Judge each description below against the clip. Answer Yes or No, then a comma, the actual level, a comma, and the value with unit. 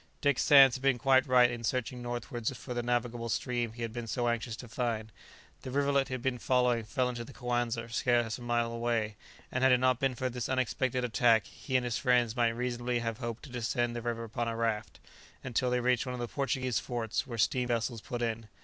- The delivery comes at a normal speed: No, fast, 230 wpm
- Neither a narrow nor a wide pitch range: No, narrow, 1.5 semitones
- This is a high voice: No, low, 120 Hz